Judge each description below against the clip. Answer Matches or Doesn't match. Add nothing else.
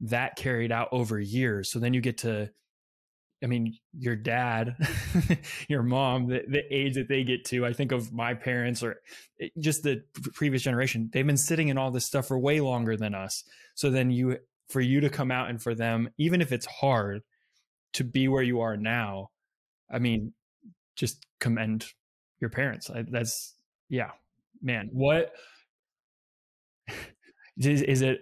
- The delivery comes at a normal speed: Matches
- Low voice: Matches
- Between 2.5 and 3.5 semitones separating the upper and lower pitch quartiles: Matches